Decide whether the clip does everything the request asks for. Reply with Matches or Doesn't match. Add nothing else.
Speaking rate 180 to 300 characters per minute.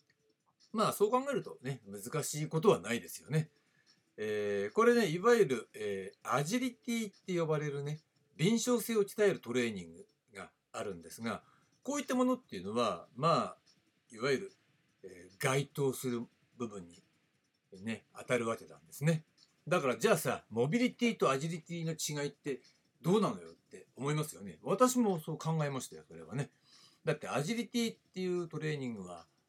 Doesn't match